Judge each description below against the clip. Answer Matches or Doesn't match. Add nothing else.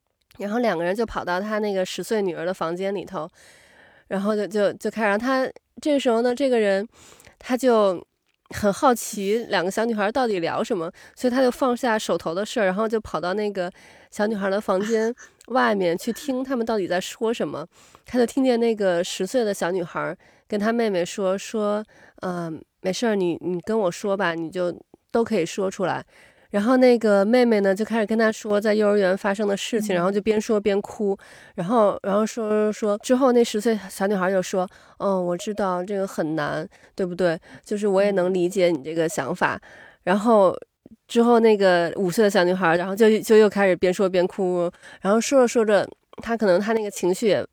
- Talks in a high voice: Matches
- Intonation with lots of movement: Doesn't match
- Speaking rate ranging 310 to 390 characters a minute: Doesn't match